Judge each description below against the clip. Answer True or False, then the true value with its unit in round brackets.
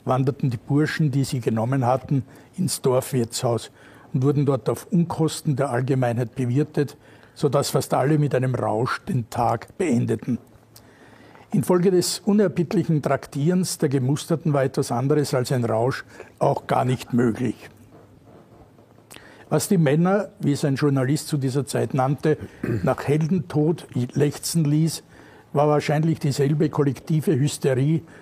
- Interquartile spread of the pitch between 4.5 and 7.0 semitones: False (3.4 semitones)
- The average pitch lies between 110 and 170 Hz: True (140 Hz)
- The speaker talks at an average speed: True (135 wpm)